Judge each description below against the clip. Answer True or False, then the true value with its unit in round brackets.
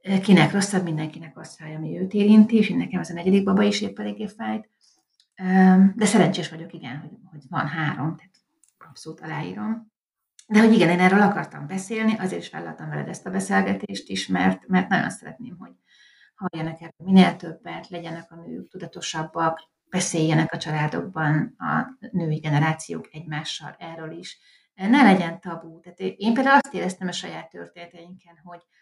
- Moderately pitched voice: True (175 Hz)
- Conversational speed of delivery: False (160 wpm)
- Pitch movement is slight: False (3.5 semitones)